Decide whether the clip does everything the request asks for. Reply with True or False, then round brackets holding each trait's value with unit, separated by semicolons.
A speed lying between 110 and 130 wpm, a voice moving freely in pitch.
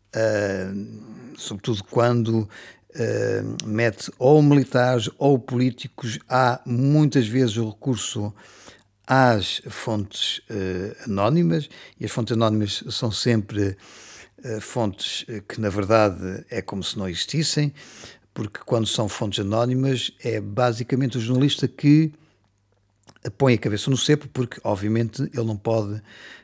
False (125 wpm; 4.0 semitones)